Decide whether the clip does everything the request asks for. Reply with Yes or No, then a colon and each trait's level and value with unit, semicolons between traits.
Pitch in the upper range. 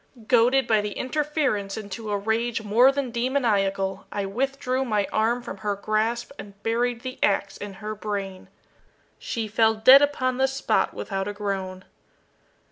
Yes: high, 220 Hz